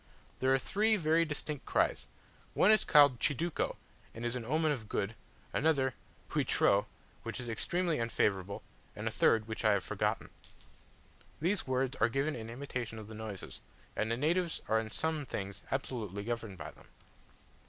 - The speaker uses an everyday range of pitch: No, wide, 5.7 semitones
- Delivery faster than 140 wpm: Yes, average, 165 wpm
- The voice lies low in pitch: Yes, low, 125 Hz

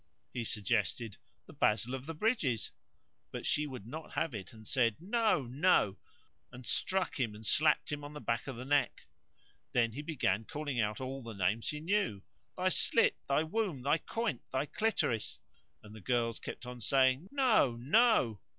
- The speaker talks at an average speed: Yes, average, 180 wpm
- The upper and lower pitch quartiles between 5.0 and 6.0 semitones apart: Yes, wide, 5.5 semitones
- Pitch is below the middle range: Yes, low, 130 Hz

